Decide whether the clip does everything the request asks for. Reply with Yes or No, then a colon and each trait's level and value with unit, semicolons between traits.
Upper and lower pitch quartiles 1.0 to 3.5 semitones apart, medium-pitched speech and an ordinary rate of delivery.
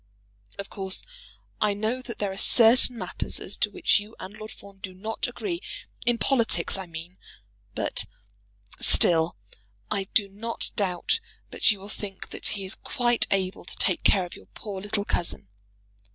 No: average, 2.8 semitones; high, 200 Hz; average, 170 wpm